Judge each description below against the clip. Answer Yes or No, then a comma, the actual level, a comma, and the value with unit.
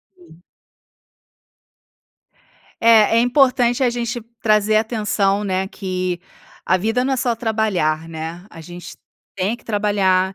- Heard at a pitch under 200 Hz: No, high, 210 Hz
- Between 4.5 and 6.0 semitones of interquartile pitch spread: No, average, 4.0 semitones